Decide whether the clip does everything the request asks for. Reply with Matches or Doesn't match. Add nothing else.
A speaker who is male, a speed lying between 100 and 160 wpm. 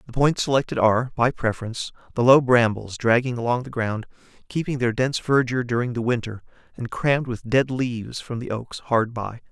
Doesn't match